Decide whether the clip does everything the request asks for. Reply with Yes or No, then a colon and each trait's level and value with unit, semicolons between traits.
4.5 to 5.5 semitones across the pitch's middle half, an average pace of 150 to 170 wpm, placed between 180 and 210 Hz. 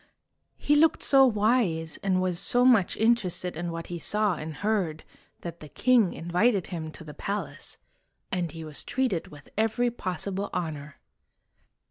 Yes: average, 5.2 semitones; average, 155 wpm; medium, 185 Hz